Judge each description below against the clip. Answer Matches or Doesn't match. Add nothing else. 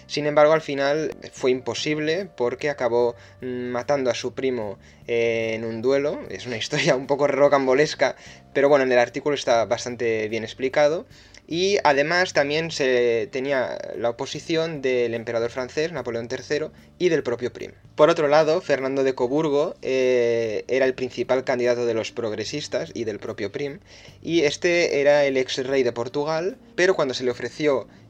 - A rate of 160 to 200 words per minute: Matches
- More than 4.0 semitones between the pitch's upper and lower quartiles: Doesn't match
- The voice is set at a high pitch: Doesn't match